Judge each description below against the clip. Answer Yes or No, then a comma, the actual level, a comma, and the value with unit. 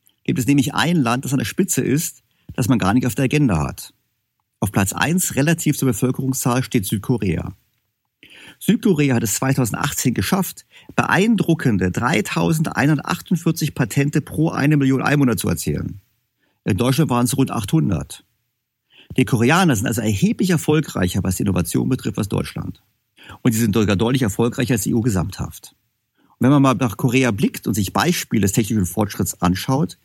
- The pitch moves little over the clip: No, average, 4.3 semitones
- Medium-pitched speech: No, low, 130 Hz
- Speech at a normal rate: Yes, average, 165 wpm